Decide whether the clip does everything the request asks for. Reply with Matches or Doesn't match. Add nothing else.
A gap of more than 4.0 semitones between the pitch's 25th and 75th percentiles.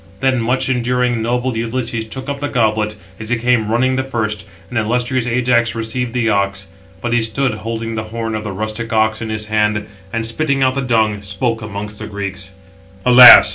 Doesn't match